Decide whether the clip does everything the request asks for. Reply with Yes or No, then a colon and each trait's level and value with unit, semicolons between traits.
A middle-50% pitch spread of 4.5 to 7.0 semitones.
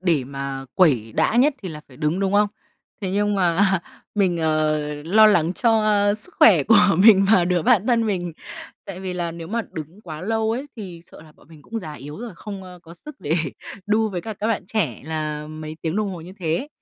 Yes: average, 5.1 semitones